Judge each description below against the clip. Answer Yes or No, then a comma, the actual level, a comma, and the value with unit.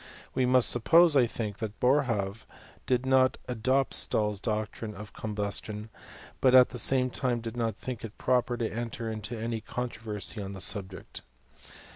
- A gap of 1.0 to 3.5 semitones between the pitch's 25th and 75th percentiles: Yes, average, 3.0 semitones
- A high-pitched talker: No, low, 115 Hz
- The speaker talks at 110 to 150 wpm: No, average, 165 wpm